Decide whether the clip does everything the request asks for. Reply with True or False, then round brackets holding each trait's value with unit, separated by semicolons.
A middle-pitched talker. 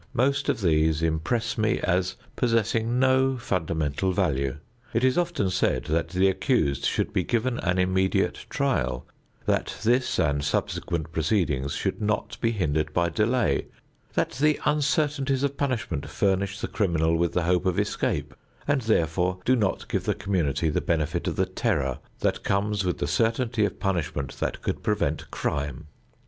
False (95 Hz)